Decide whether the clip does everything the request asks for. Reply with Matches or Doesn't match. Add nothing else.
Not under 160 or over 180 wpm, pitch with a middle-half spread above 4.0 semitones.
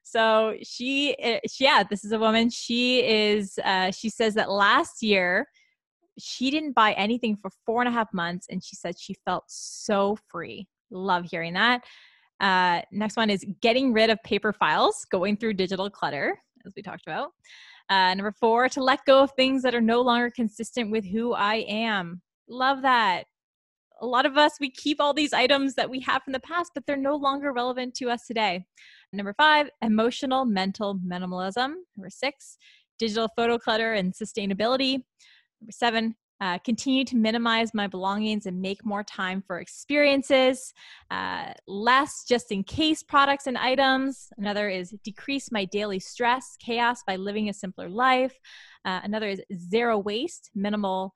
Matches